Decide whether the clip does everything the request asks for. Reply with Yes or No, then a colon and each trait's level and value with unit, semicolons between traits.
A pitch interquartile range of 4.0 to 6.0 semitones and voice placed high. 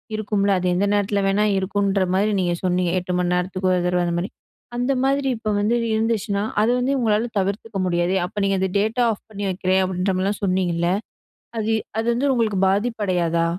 No: average, 2.9 semitones; high, 200 Hz